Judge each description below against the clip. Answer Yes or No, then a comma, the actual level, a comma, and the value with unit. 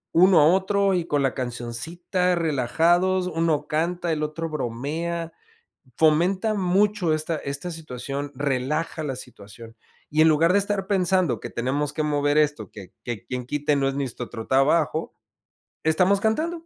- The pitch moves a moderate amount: Yes, average, 4.3 semitones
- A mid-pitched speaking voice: Yes, medium, 155 Hz